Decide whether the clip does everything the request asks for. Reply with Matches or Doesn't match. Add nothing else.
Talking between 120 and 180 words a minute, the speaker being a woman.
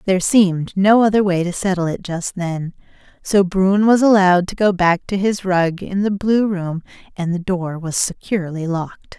Doesn't match